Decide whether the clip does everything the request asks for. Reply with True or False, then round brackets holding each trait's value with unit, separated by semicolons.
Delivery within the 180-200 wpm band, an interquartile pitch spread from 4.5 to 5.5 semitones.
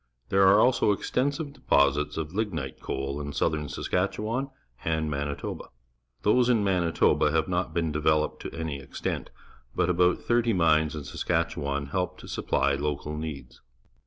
False (150 wpm; 5.2 semitones)